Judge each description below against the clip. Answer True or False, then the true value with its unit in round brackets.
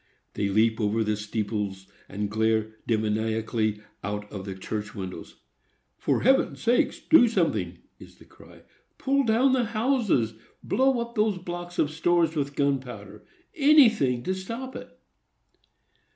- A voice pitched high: False (125 Hz)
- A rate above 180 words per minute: False (135 wpm)